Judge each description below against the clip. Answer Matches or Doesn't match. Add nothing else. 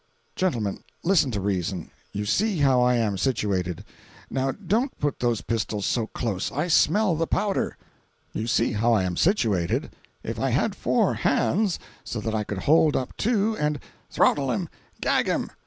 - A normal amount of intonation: Doesn't match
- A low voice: Matches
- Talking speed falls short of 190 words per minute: Matches